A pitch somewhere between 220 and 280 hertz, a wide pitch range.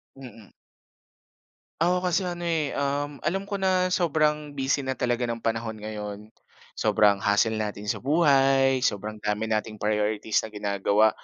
No: low, 125 Hz; wide, 6.0 semitones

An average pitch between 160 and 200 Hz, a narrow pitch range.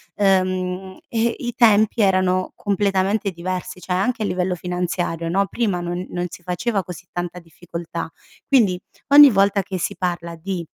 Yes: medium, 185 Hz; narrow, 2.0 semitones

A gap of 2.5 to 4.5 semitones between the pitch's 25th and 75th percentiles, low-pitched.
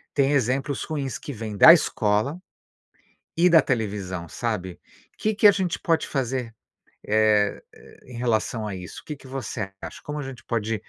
No: wide, 5.4 semitones; low, 125 Hz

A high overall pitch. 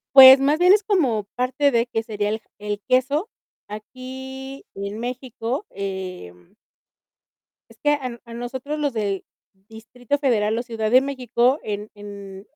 Yes: high, 240 Hz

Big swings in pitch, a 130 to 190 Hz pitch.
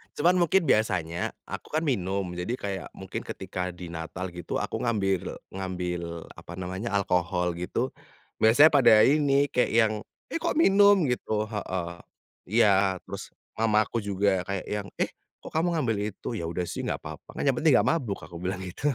No: wide, 5.7 semitones; low, 100 Hz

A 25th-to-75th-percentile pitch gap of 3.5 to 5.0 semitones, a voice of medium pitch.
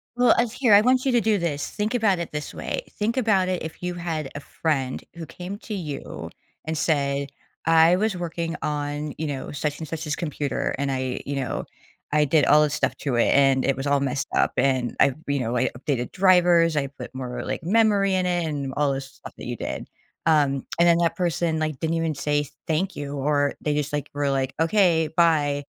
Yes: average, 3.8 semitones; medium, 155 Hz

